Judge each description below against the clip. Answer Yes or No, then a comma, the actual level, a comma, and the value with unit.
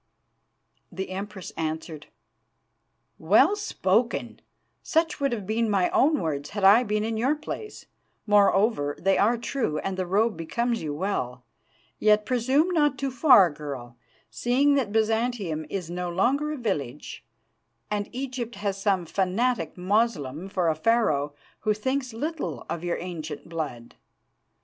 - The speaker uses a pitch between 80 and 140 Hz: No, high, 205 Hz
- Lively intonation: Yes, wide, 6.2 semitones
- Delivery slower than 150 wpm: Yes, average, 140 wpm